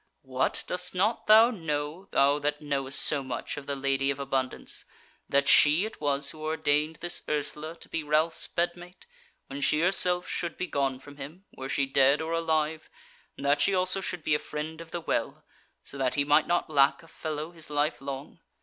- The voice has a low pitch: No, medium, 150 Hz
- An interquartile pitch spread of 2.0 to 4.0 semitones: Yes, average, 3.0 semitones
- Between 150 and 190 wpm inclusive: No, average, 200 wpm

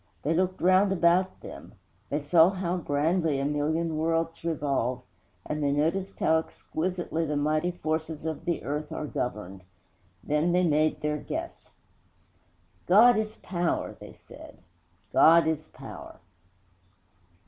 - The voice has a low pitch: No, medium, 160 Hz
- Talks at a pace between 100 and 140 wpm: Yes, slow, 135 wpm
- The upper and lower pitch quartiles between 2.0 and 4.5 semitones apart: Yes, average, 2.9 semitones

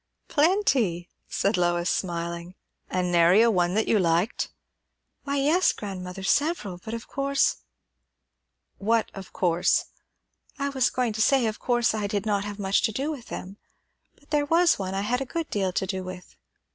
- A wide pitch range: Yes, wide, 6.4 semitones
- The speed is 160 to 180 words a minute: Yes, average, 175 wpm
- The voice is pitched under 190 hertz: No, high, 205 Hz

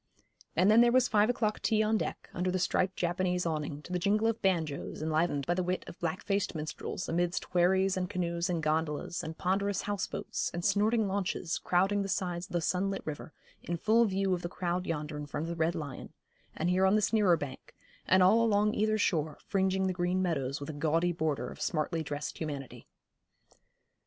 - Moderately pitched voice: Yes, medium, 180 Hz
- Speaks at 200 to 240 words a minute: Yes, fast, 205 wpm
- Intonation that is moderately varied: Yes, average, 3.5 semitones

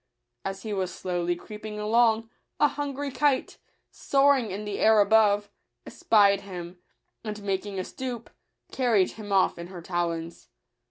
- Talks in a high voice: Yes, high, 205 Hz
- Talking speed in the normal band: Yes, average, 145 wpm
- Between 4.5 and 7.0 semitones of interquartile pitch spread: No, average, 3.4 semitones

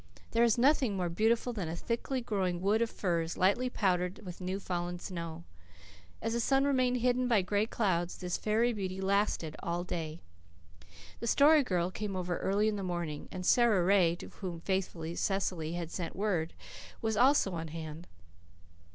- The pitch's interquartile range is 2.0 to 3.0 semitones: No, average, 4.5 semitones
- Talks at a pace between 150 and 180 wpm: Yes, average, 175 wpm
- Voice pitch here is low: No, high, 190 Hz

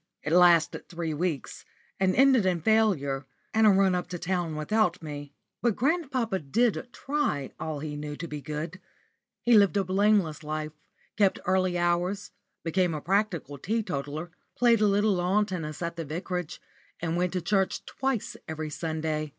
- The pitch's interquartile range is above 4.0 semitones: Yes, average, 4.9 semitones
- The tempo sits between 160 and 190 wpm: Yes, average, 165 wpm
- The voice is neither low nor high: Yes, medium, 180 Hz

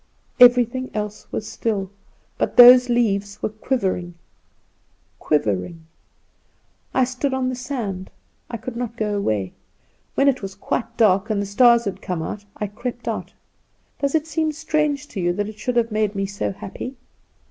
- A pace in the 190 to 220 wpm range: No, average, 160 wpm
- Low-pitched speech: No, high, 225 Hz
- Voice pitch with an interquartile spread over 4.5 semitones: No, average, 4.2 semitones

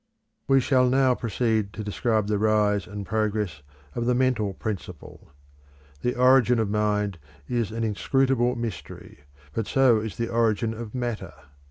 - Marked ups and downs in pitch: No, average, 2.8 semitones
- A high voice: No, low, 110 Hz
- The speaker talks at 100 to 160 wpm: Yes, average, 150 wpm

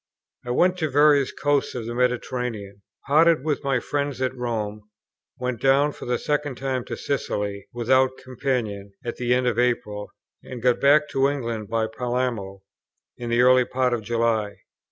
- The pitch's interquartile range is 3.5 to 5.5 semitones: No, average, 2.9 semitones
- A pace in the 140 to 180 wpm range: Yes, average, 170 wpm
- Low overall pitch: Yes, low, 125 Hz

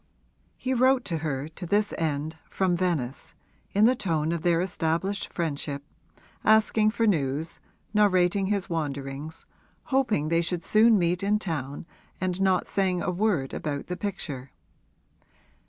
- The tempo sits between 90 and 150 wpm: Yes, average, 140 wpm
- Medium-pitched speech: Yes, medium, 175 Hz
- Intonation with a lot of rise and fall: No, average, 4.6 semitones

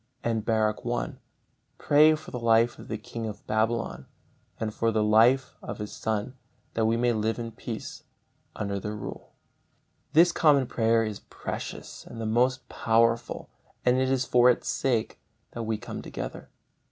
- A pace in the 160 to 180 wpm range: Yes, average, 165 wpm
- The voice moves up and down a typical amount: No, narrow, 2.0 semitones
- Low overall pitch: Yes, low, 115 Hz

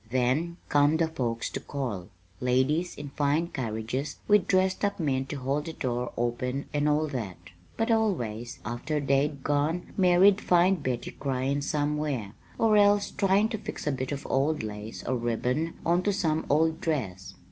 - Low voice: No, medium, 145 Hz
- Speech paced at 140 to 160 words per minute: No, average, 170 wpm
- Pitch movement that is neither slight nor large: Yes, average, 5.0 semitones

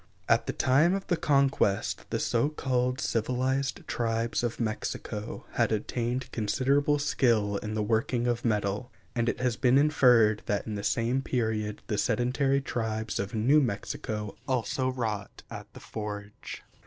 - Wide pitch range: No, average, 3.4 semitones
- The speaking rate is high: No, average, 155 wpm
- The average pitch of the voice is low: Yes, low, 120 Hz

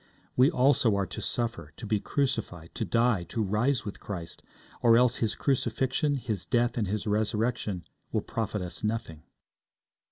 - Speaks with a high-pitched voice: No, low, 115 Hz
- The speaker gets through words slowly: No, average, 160 wpm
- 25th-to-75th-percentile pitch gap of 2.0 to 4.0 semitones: Yes, average, 3.3 semitones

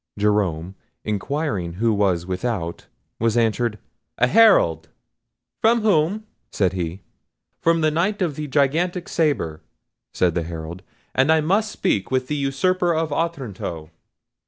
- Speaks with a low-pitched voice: Yes, low, 125 Hz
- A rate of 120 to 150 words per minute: Yes, slow, 135 wpm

